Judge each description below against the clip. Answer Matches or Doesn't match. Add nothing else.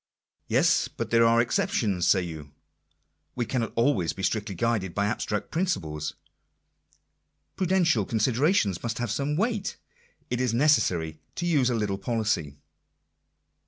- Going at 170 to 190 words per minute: Doesn't match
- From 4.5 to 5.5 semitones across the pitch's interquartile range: Matches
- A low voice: Matches